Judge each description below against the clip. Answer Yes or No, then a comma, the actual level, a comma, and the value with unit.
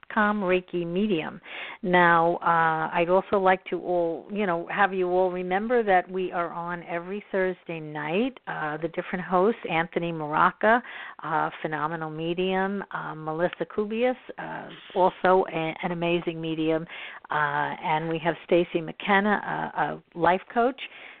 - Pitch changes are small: Yes, narrow, 2.2 semitones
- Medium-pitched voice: Yes, medium, 180 Hz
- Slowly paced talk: No, average, 145 wpm